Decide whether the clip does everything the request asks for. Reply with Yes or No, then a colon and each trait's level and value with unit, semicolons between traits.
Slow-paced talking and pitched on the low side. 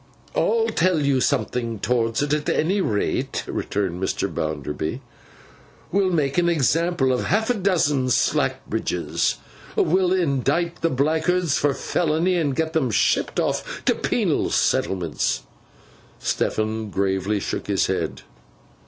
No: slow, 130 wpm; medium, 145 Hz